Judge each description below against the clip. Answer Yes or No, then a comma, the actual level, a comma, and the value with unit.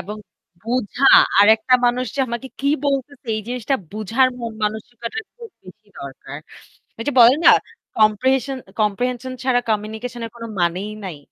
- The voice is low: No, high, 230 Hz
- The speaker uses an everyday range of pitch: Yes, average, 3.3 semitones